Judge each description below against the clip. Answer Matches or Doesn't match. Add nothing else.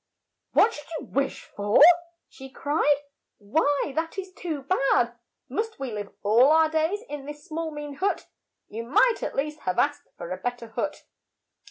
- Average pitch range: Matches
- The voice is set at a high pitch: Matches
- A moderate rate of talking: Matches